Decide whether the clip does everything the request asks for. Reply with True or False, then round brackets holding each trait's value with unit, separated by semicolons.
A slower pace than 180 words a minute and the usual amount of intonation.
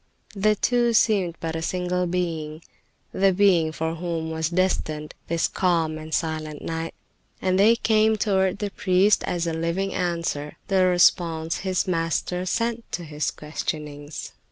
True (150 wpm; 3.0 semitones)